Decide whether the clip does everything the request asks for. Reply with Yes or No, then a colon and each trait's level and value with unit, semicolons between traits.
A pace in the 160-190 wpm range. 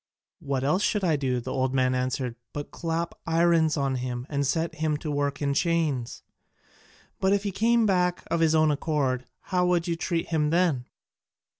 Yes: average, 185 wpm